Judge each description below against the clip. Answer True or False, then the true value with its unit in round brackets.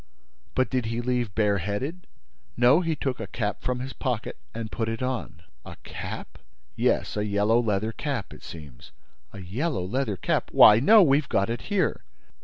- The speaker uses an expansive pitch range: False (4.2 semitones)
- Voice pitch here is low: True (115 Hz)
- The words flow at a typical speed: True (180 wpm)